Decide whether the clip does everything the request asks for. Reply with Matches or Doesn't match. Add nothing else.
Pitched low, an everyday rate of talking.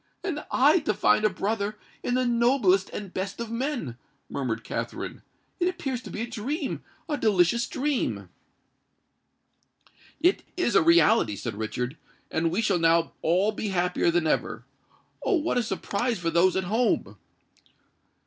Doesn't match